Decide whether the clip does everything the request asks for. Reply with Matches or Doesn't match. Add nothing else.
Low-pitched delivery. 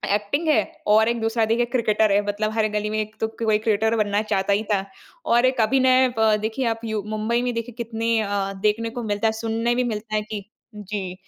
Doesn't match